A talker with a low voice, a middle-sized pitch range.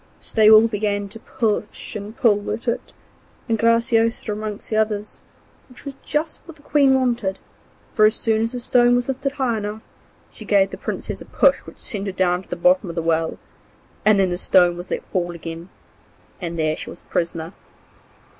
No: high, 215 Hz; average, 3.9 semitones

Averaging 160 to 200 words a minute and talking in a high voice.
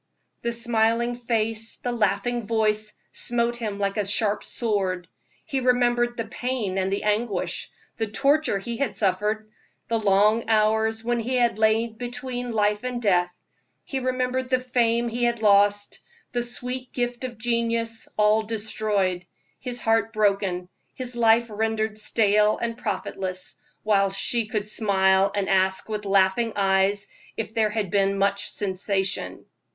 No: average, 145 wpm; high, 220 Hz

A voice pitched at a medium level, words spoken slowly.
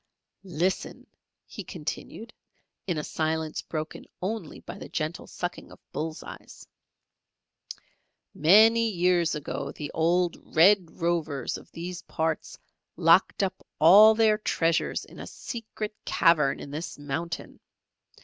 Yes: medium, 170 Hz; slow, 120 wpm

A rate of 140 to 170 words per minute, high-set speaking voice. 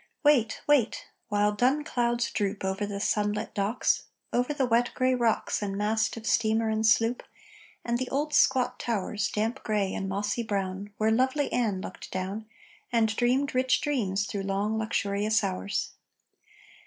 Yes: average, 155 wpm; high, 220 Hz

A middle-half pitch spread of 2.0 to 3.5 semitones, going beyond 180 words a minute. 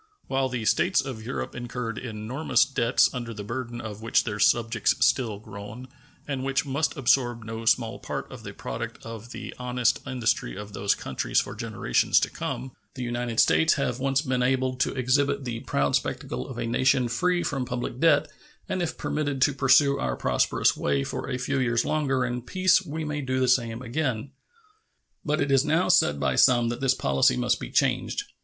Yes: average, 3.1 semitones; average, 190 wpm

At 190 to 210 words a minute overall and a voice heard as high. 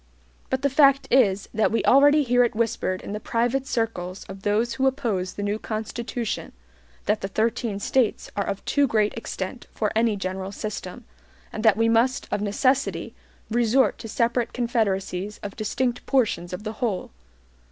No: average, 170 wpm; high, 225 Hz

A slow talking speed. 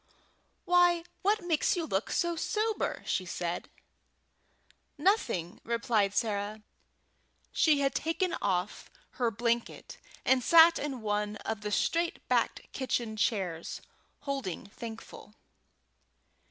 Yes: slow, 110 wpm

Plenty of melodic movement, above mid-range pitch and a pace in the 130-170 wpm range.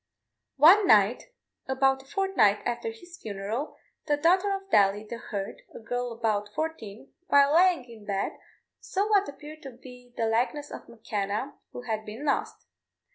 Yes: wide, 6.0 semitones; very high, 250 Hz; average, 160 wpm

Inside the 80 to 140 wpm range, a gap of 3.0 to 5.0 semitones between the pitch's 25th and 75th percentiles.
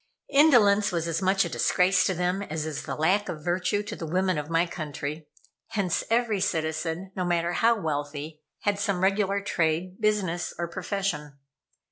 No: average, 170 wpm; average, 3.8 semitones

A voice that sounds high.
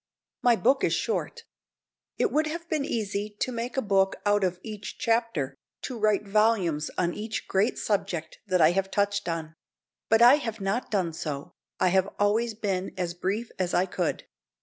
Yes: high, 205 Hz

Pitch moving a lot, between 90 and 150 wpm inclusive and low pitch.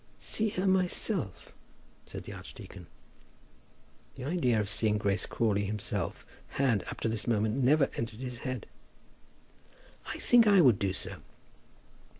Yes: wide, 6.6 semitones; average, 140 wpm; low, 120 Hz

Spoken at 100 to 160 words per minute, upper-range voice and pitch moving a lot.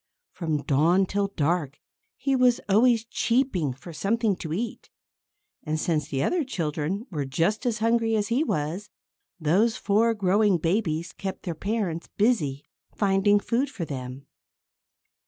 Yes: average, 140 wpm; high, 195 Hz; wide, 6.3 semitones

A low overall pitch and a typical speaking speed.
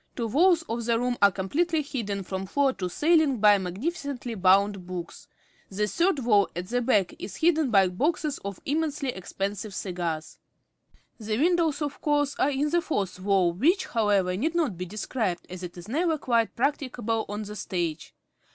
No: high, 225 Hz; average, 175 wpm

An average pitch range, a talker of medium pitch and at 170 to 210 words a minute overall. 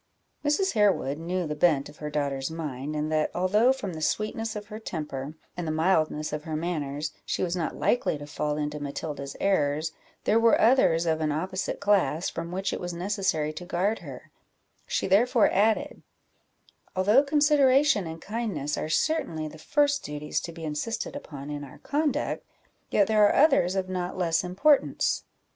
No: wide, 5.8 semitones; medium, 175 Hz; average, 175 wpm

